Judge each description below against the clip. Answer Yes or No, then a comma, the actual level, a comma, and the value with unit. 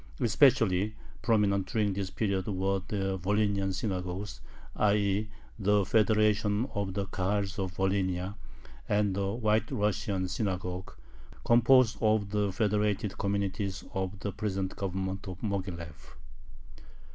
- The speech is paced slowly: Yes, slow, 120 wpm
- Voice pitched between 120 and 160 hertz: No, low, 100 Hz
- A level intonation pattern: Yes, narrow, 1.9 semitones